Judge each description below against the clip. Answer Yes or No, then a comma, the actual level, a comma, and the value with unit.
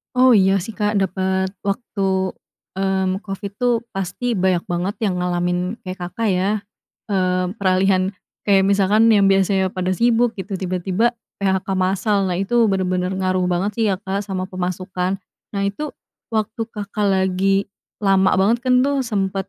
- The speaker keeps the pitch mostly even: Yes, narrow, 1.9 semitones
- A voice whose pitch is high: Yes, high, 195 Hz